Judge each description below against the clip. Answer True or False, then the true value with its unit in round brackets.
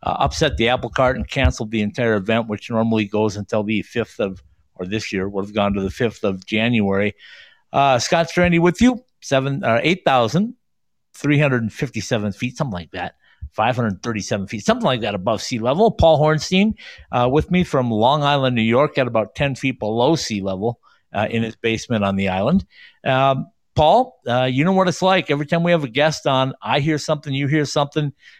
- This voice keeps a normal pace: False (215 wpm)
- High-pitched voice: False (125 Hz)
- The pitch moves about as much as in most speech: False (6.0 semitones)